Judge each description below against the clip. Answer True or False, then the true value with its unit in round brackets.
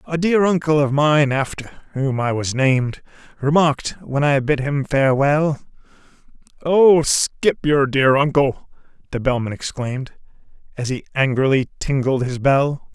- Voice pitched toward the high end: False (140 Hz)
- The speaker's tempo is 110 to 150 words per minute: True (140 wpm)